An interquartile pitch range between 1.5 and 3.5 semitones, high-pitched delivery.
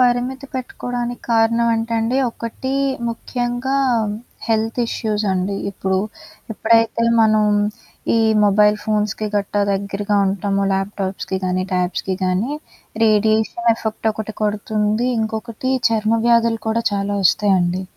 Yes: narrow, 2.5 semitones; high, 220 Hz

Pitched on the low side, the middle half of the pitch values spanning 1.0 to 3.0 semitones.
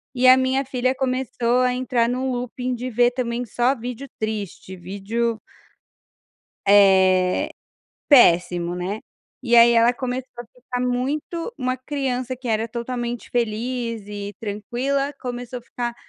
No: high, 245 Hz; narrow, 2.6 semitones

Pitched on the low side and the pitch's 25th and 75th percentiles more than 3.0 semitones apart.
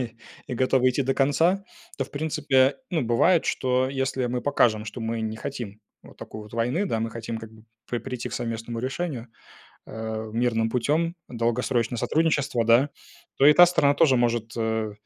Yes: low, 125 Hz; average, 3.5 semitones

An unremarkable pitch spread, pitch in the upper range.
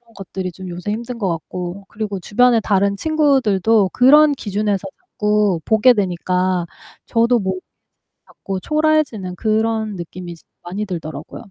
Yes: average, 3.8 semitones; high, 205 Hz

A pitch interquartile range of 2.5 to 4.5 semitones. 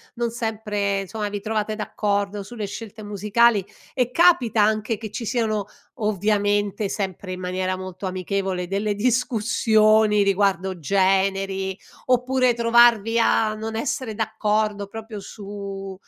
No: narrow, 2.1 semitones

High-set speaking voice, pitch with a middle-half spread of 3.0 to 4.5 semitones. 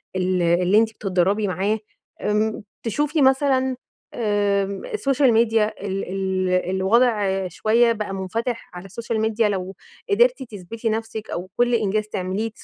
Yes: high, 215 Hz; average, 3.4 semitones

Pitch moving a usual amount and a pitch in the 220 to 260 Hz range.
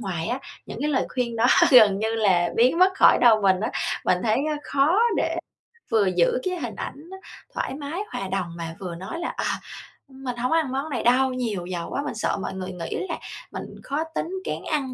No: wide, 6.5 semitones; high, 235 Hz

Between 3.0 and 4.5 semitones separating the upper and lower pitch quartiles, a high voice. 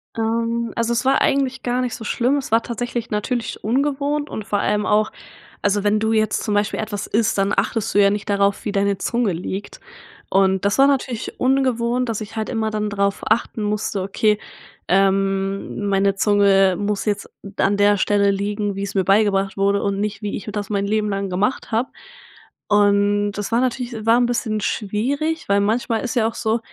No: narrow, 2.6 semitones; high, 210 Hz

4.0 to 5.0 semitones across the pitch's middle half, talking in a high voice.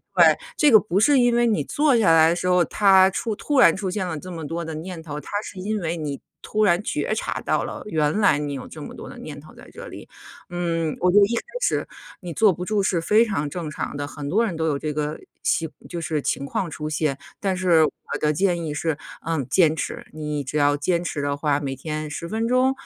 No: average, 4.7 semitones; medium, 170 Hz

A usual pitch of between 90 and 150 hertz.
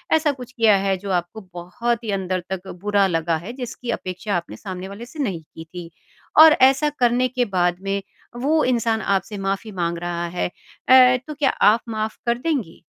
No: high, 205 Hz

